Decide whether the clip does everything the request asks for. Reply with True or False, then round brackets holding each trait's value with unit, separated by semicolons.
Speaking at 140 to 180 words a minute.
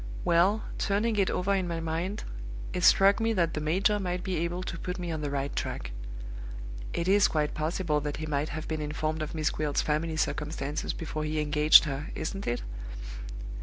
False (195 wpm)